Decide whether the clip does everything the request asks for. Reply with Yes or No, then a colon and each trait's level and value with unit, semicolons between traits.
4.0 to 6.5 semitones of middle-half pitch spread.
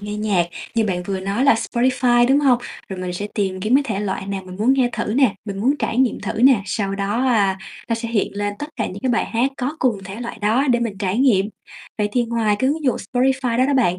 Yes: average, 4.3 semitones